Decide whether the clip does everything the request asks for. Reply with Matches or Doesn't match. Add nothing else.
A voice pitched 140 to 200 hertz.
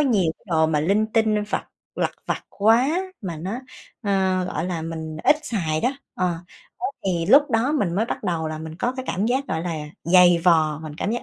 Matches